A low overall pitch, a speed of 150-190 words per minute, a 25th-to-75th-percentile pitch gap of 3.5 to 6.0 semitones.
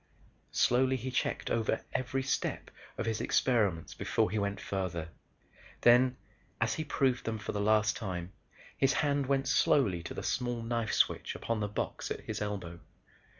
Yes: low, 115 Hz; average, 165 wpm; average, 4.2 semitones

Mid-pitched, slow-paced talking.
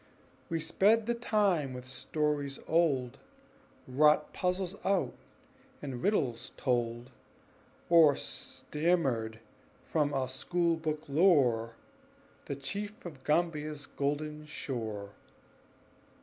Yes: medium, 150 Hz; slow, 95 wpm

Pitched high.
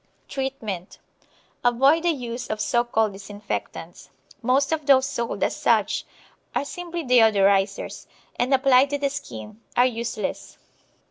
Yes: high, 245 Hz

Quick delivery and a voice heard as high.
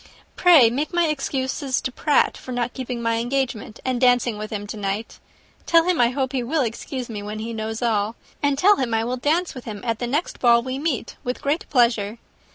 Yes: fast, 220 wpm; high, 245 Hz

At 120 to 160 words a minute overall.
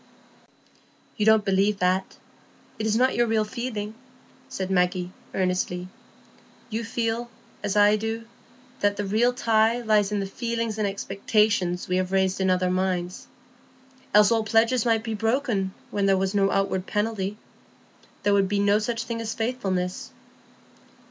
Yes: average, 155 wpm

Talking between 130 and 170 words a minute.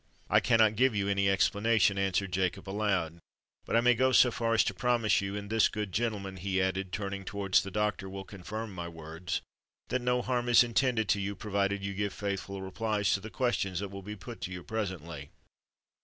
No: average, 200 wpm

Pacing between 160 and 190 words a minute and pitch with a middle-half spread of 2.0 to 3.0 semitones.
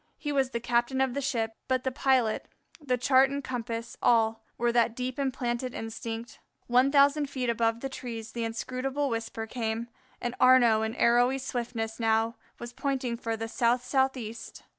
Yes: average, 170 wpm; narrow, 2.4 semitones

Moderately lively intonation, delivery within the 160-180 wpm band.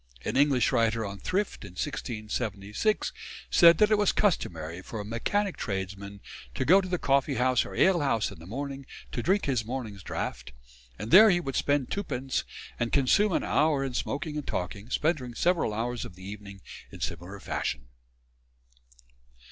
No: wide, 7.2 semitones; average, 170 wpm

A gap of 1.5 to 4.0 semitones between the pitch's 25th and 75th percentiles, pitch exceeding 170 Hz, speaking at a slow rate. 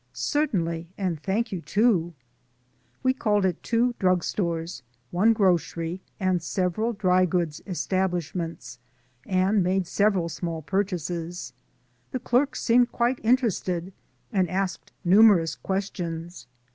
Yes: average, 3.7 semitones; medium, 185 Hz; slow, 115 wpm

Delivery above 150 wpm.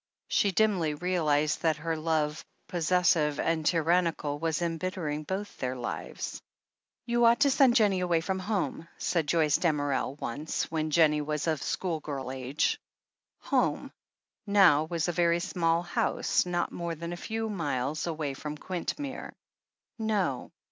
No: average, 145 wpm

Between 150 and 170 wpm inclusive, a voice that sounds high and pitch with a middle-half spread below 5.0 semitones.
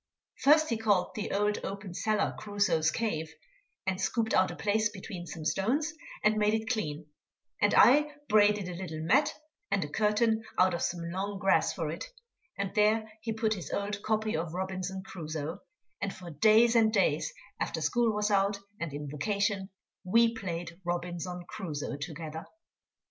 Yes: average, 165 wpm; high, 200 Hz; average, 3.9 semitones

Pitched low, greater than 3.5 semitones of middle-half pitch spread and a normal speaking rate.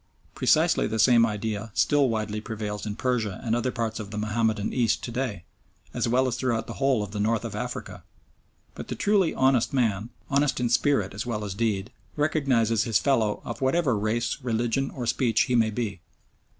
No: low, 115 Hz; average, 3.0 semitones; average, 190 wpm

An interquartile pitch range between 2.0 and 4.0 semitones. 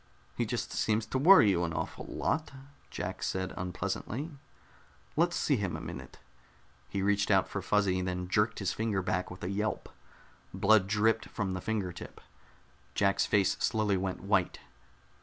Yes: average, 2.7 semitones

